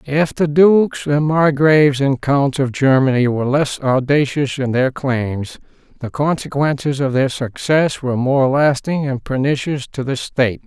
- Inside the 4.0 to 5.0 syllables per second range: Yes, 4.4 syllables/s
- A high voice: No, medium, 140 Hz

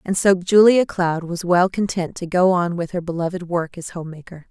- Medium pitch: Yes, medium, 175 Hz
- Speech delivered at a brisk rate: Yes, fast, 225 wpm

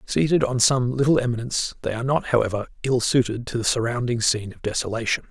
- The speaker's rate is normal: Yes, average, 190 wpm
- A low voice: Yes, low, 120 Hz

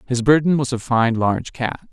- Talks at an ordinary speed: No, fast, 220 wpm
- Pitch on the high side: No, low, 125 Hz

